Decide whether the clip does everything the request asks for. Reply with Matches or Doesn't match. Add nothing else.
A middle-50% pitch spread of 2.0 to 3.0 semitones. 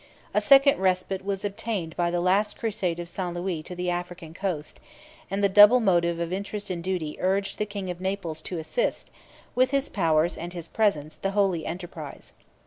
Matches